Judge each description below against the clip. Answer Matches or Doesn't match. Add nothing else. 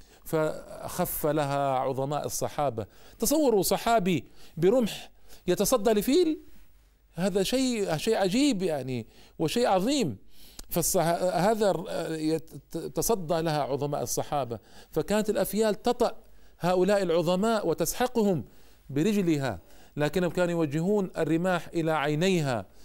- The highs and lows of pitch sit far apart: Matches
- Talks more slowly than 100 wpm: Matches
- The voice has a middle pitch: Matches